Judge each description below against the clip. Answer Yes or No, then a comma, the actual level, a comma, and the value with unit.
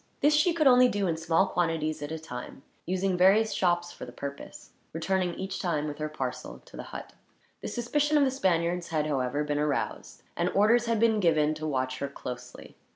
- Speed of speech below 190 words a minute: No, fast, 205 wpm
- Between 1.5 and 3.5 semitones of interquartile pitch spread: No, wide, 5.4 semitones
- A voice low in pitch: No, medium, 170 Hz